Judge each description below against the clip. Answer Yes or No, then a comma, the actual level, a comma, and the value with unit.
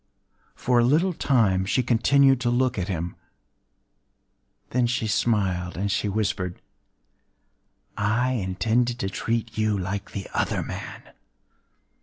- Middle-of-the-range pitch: No, low, 110 Hz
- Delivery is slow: Yes, slow, 115 wpm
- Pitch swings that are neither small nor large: Yes, average, 4.2 semitones